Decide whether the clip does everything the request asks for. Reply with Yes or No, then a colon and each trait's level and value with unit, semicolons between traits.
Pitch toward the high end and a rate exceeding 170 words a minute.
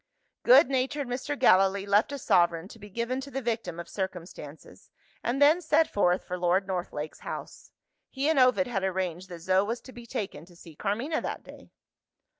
Yes: high, 205 Hz; average, 190 wpm